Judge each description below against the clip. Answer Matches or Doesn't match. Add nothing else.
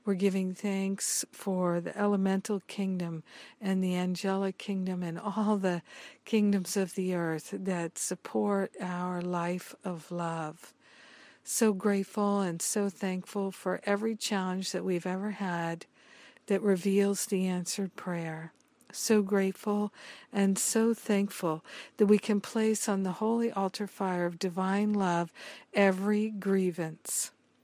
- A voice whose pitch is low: Doesn't match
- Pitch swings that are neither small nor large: Doesn't match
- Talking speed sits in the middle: Doesn't match